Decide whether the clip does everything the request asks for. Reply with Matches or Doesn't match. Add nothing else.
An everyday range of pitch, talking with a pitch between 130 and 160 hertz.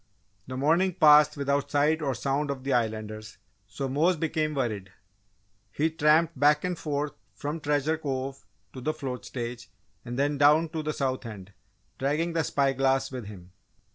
Matches